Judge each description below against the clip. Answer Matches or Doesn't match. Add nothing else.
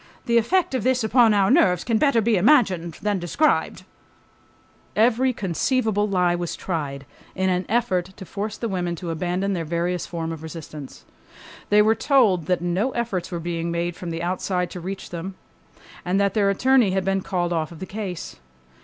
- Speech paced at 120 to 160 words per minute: Doesn't match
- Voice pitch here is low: Doesn't match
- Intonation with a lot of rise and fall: Doesn't match